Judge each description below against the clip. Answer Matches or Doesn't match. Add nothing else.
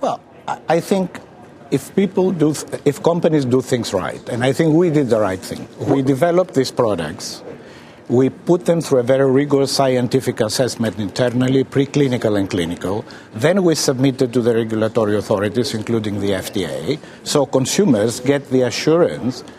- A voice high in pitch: Doesn't match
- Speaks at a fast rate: Doesn't match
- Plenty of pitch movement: Doesn't match